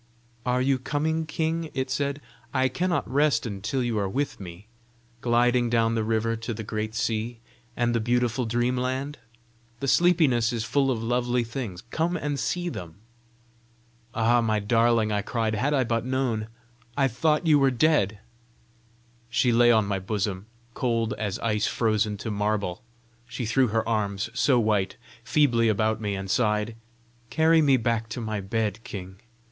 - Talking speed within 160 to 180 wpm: Yes, average, 165 wpm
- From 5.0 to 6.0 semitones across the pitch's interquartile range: No, average, 3.3 semitones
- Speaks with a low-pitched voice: Yes, low, 115 Hz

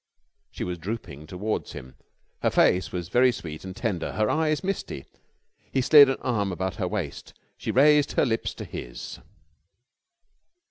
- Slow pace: No, average, 155 wpm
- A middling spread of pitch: No, wide, 6.5 semitones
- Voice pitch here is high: No, low, 100 Hz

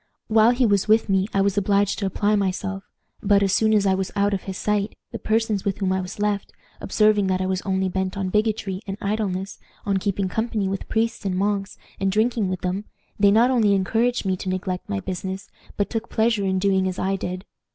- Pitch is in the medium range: No, high, 200 Hz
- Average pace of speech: No, fast, 225 wpm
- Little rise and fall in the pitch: Yes, narrow, 1.9 semitones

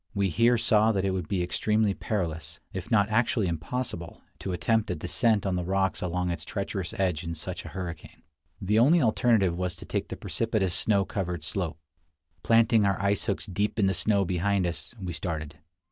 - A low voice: Yes, very low, 95 Hz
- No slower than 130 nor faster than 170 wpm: No, average, 190 wpm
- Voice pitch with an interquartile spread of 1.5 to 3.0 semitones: No, average, 3.4 semitones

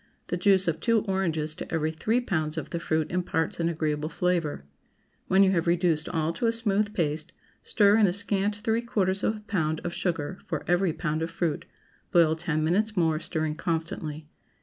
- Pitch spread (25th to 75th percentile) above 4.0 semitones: No, average, 3.7 semitones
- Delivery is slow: No, average, 195 wpm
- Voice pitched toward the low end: No, medium, 170 Hz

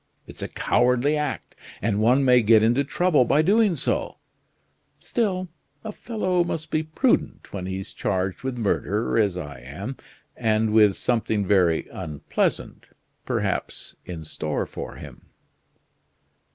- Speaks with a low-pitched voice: Yes, low, 115 Hz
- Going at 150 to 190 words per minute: No, slow, 135 wpm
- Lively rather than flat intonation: Yes, wide, 7.7 semitones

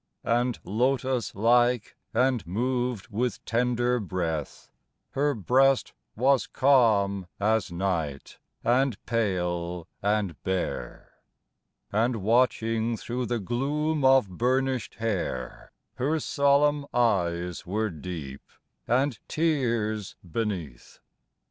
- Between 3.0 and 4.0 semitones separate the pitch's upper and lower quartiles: No, average, 4.9 semitones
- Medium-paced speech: No, slow, 95 wpm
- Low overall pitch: Yes, low, 115 Hz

